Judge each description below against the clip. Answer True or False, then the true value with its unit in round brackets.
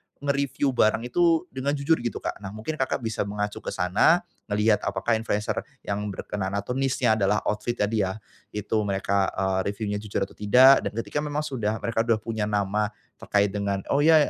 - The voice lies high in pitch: False (110 Hz)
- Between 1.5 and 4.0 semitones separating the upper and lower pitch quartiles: False (4.5 semitones)